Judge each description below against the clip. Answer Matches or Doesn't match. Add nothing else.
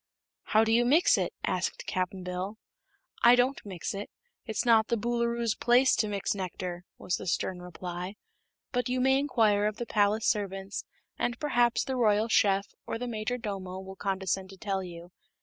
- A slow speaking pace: Doesn't match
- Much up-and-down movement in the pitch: Doesn't match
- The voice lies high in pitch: Matches